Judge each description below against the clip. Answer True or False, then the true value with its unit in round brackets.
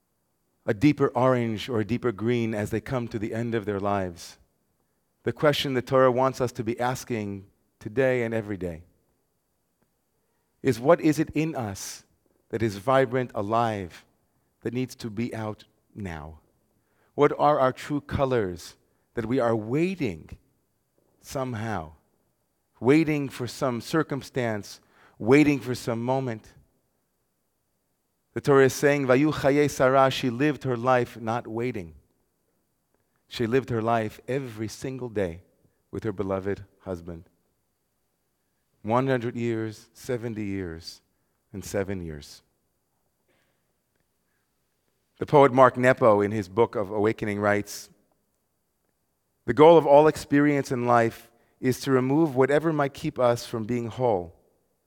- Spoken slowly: True (130 wpm)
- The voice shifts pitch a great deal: False (4.2 semitones)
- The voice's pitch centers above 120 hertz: False (115 Hz)